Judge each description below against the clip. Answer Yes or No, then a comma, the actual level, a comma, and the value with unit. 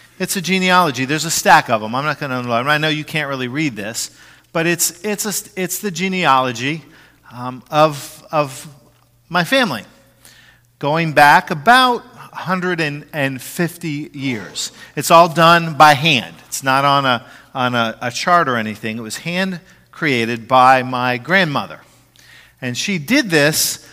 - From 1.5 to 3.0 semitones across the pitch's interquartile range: No, average, 5.0 semitones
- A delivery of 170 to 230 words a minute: No, average, 155 wpm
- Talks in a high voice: No, medium, 150 Hz